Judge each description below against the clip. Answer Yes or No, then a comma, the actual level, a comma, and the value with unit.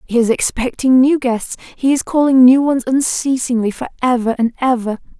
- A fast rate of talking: No, average, 175 wpm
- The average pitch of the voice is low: No, very high, 250 Hz